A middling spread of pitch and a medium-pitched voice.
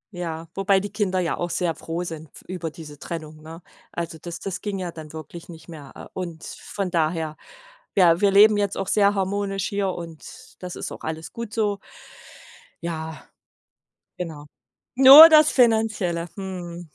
Yes: average, 3.5 semitones; medium, 175 Hz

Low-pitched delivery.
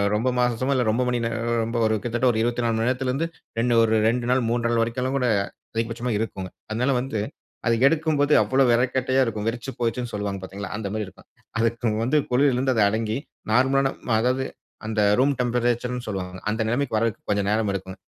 Yes: low, 120 Hz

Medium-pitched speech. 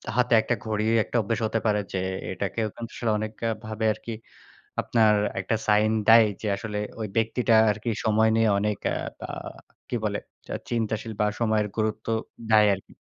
No: low, 110 Hz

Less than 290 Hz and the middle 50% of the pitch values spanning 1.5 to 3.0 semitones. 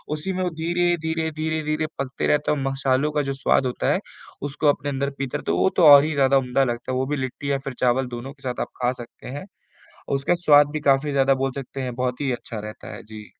Yes: medium, 140 Hz; average, 2.7 semitones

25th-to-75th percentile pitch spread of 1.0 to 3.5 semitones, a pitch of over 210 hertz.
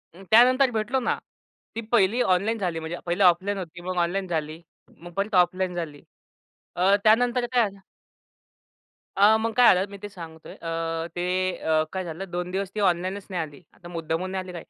No: average, 2.9 semitones; medium, 185 Hz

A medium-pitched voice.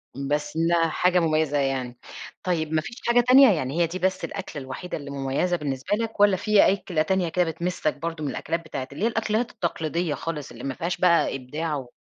Yes: medium, 165 Hz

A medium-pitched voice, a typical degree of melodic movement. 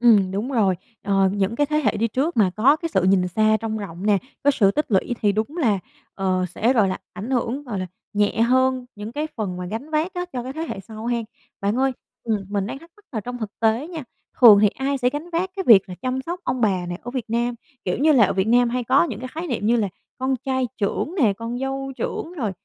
No: high, 235 Hz; average, 4.7 semitones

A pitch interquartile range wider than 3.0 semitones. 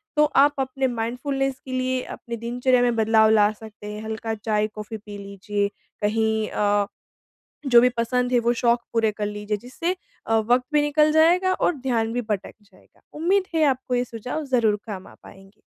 Yes: average, 3.5 semitones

